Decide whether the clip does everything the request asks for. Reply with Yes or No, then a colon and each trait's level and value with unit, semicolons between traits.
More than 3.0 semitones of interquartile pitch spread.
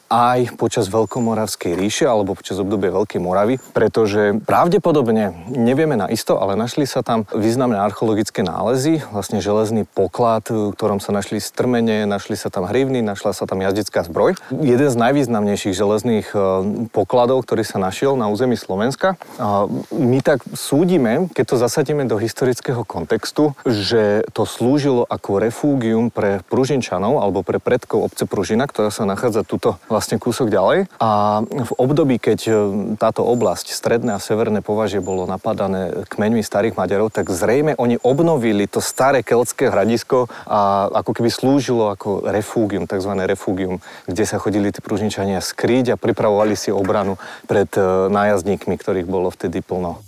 Yes: average, 3.4 semitones